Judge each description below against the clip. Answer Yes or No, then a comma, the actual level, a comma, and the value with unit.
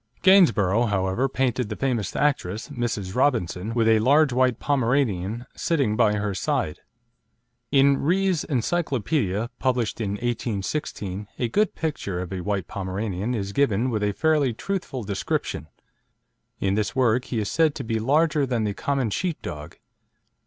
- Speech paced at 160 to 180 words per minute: No, average, 150 wpm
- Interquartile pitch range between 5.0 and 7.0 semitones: Yes, wide, 5.4 semitones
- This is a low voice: Yes, low, 115 Hz